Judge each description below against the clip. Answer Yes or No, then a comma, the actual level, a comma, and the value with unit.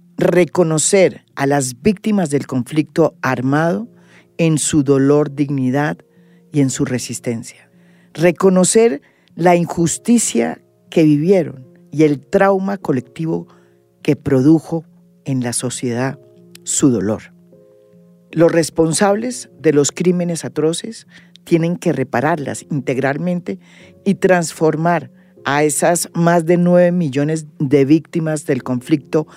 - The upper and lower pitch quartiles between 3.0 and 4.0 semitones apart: No, average, 4.6 semitones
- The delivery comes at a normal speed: No, slow, 110 wpm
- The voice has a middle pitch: Yes, medium, 155 Hz